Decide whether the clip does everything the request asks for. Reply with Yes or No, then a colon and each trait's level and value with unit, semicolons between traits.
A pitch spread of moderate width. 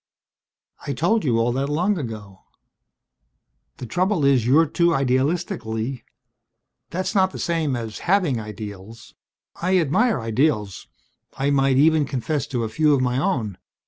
No: wide, 6.2 semitones